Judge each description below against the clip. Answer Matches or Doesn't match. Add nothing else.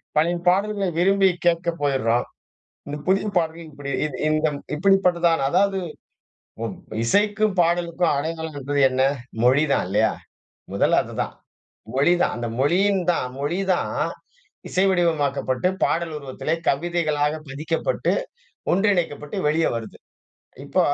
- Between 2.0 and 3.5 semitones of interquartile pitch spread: Doesn't match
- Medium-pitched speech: Matches